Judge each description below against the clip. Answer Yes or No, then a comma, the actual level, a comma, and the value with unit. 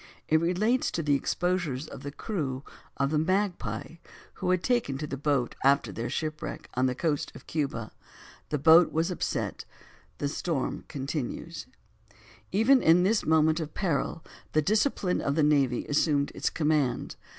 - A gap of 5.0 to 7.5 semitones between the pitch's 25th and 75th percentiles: No, average, 4.1 semitones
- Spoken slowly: No, average, 160 wpm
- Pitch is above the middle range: No, medium, 155 Hz